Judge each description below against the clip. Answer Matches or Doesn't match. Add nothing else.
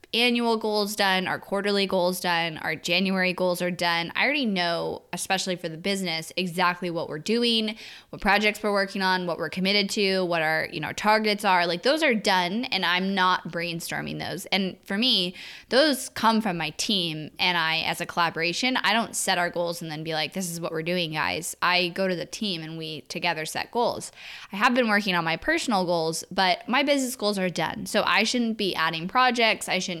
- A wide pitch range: Doesn't match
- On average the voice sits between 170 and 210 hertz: Matches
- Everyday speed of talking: Doesn't match